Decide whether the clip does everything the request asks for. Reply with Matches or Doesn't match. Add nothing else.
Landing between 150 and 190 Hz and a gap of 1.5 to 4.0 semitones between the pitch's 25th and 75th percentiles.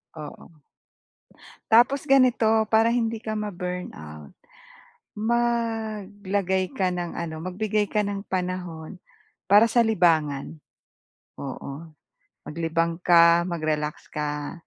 Doesn't match